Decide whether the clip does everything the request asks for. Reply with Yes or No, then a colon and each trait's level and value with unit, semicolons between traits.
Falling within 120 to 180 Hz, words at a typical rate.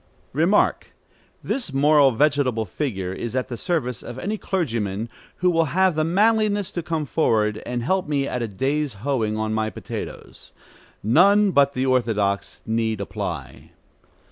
Yes: low, 135 Hz; average, 150 wpm